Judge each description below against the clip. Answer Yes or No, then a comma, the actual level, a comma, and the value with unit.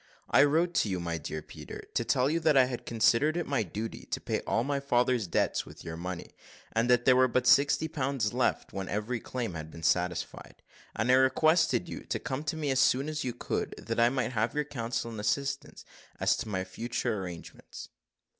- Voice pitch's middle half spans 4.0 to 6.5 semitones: Yes, average, 4.8 semitones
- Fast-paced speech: Yes, fast, 215 wpm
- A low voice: Yes, low, 125 Hz